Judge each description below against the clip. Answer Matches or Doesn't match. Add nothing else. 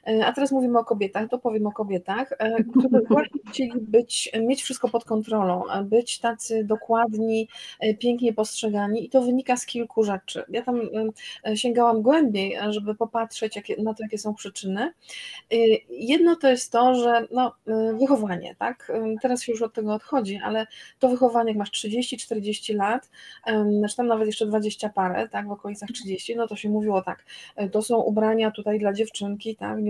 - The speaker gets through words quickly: Matches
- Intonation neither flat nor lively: Doesn't match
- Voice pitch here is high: Matches